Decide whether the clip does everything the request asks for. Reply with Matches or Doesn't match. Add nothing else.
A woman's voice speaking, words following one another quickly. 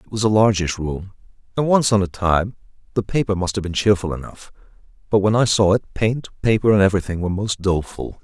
Doesn't match